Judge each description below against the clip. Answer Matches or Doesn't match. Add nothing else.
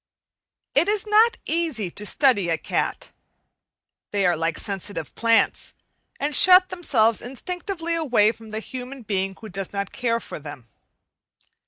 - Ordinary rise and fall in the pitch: Doesn't match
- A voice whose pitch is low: Doesn't match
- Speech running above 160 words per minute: Doesn't match